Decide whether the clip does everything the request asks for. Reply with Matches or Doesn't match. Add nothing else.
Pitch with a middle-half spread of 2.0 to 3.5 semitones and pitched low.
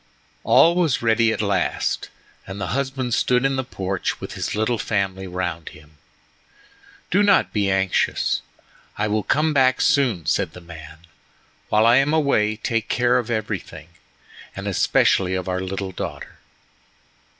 Doesn't match